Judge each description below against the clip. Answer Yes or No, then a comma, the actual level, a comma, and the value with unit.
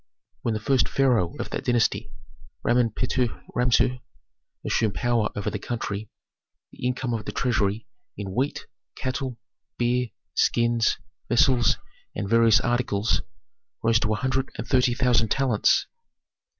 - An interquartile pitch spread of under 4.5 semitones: Yes, narrow, 2.5 semitones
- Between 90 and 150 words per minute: Yes, slow, 135 wpm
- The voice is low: Yes, low, 120 Hz